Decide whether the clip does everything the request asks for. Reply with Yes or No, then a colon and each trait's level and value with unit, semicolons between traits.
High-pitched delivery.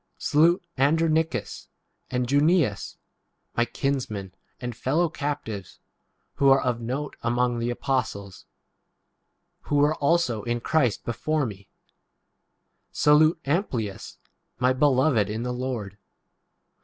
No: low, 130 Hz